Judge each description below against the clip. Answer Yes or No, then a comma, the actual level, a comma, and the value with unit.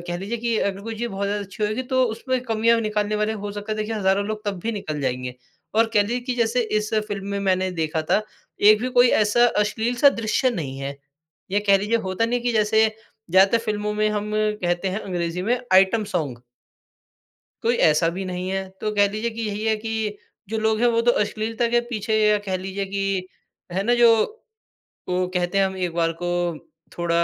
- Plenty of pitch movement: No, average, 3.1 semitones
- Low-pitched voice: No, high, 210 Hz